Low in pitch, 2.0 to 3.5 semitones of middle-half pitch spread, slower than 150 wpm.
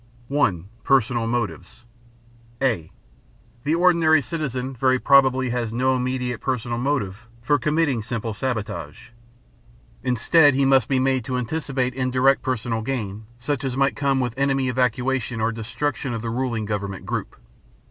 Yes: low, 125 Hz; average, 2.9 semitones; average, 140 wpm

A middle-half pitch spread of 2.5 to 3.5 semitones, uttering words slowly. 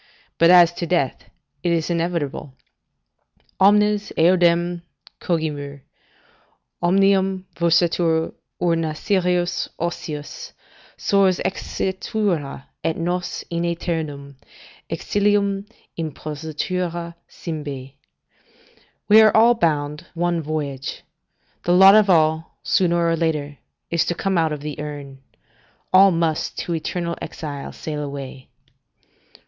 Yes: average, 3.1 semitones; slow, 105 wpm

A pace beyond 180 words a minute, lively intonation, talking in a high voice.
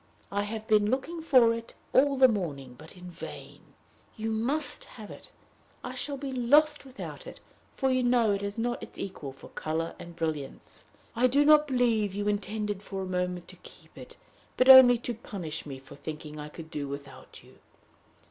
Yes: average, 190 wpm; wide, 7.2 semitones; high, 215 Hz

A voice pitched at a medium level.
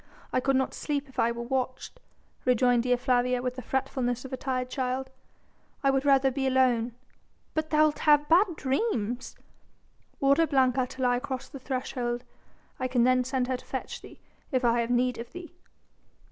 No: very high, 255 Hz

